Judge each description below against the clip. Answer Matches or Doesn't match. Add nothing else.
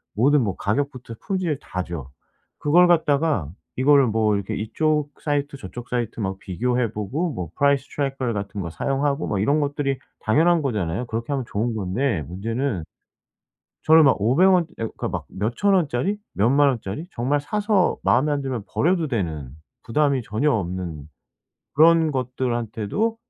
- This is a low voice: Matches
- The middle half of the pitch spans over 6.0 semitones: Doesn't match